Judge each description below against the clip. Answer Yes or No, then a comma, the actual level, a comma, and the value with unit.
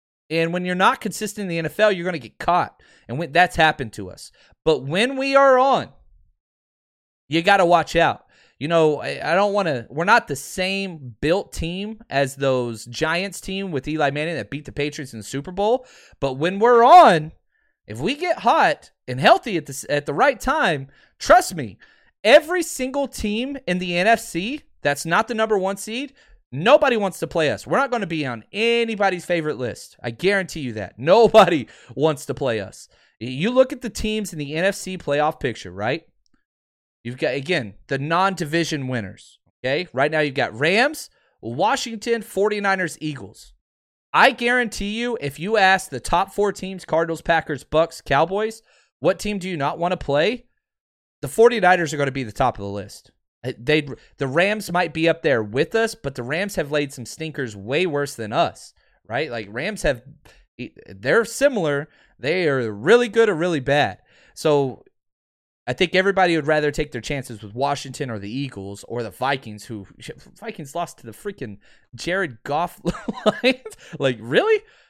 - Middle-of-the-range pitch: Yes, medium, 165 Hz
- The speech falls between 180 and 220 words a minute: Yes, average, 185 wpm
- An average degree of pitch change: No, wide, 7.2 semitones